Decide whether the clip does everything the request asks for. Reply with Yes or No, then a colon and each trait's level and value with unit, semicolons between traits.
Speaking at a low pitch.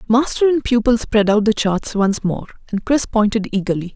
No: high, 220 Hz